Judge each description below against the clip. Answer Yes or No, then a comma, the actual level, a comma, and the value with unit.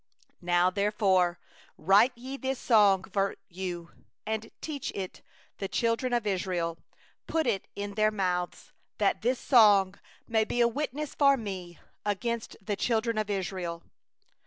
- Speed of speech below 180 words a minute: Yes, average, 145 wpm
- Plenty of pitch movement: No, average, 3.9 semitones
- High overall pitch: Yes, high, 205 Hz